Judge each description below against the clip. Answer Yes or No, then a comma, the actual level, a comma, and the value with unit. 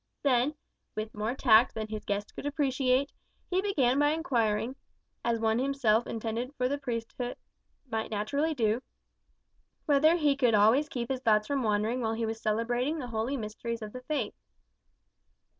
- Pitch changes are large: No, average, 4.0 semitones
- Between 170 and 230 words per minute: No, average, 160 wpm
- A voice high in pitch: Yes, high, 245 Hz